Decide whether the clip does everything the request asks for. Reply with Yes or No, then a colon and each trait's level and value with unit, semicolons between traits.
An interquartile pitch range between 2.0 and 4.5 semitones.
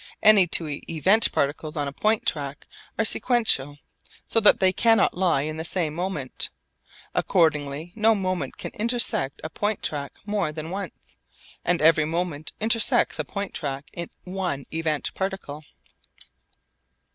No: average, 4.9 semitones